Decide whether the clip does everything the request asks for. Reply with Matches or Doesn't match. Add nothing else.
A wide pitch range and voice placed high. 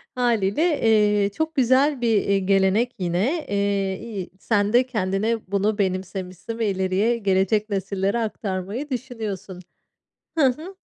Doesn't match